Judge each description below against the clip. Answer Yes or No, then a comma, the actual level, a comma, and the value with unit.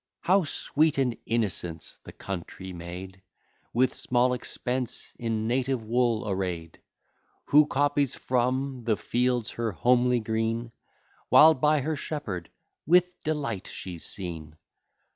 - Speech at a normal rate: No, slow, 120 wpm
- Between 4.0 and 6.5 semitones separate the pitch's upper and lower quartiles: Yes, wide, 5.6 semitones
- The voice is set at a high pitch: No, low, 120 Hz